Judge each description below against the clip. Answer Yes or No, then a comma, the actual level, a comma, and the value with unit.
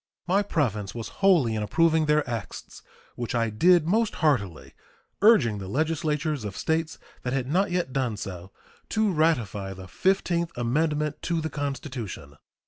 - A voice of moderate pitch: Yes, medium, 150 Hz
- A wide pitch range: Yes, wide, 6.7 semitones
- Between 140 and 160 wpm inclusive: Yes, average, 150 wpm